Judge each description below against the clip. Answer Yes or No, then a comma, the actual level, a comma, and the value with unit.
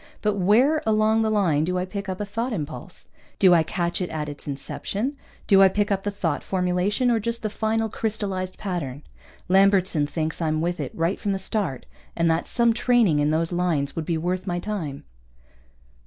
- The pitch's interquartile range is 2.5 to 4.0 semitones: No, average, 4.4 semitones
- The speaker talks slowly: No, average, 200 wpm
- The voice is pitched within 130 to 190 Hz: Yes, medium, 185 Hz